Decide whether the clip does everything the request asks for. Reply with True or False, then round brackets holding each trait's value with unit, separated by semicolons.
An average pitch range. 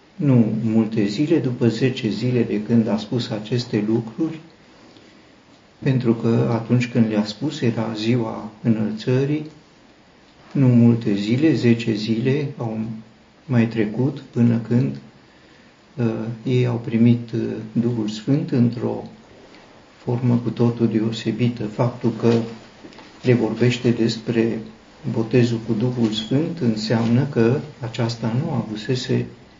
False (1.8 semitones)